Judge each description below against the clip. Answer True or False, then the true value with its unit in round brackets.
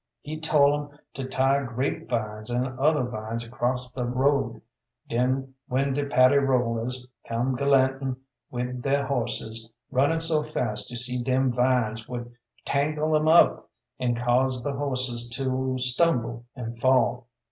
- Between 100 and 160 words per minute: True (145 wpm)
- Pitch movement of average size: False (2.3 semitones)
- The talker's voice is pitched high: False (130 Hz)